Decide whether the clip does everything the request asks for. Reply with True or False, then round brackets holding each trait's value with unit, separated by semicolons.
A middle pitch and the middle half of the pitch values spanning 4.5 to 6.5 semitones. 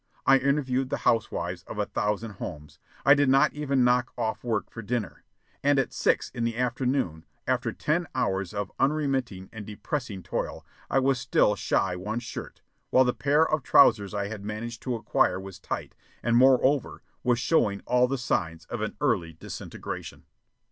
False (120 Hz; 4.8 semitones)